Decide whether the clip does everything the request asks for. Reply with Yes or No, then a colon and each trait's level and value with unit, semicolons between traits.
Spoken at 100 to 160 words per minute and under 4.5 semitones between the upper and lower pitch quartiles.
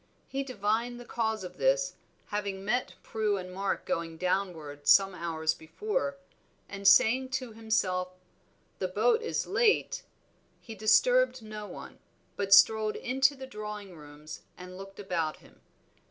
No: average, 140 wpm; average, 5.0 semitones